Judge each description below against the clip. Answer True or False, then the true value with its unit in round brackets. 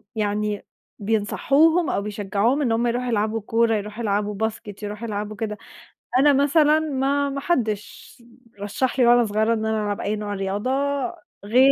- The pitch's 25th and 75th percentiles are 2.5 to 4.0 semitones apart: True (3.5 semitones)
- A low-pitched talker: False (220 Hz)